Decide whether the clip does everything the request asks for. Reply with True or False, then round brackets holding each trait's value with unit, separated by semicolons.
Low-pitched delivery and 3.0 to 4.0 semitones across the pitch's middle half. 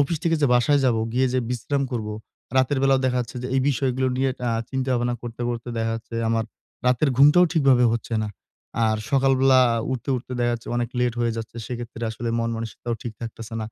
False (125 Hz; 2.4 semitones)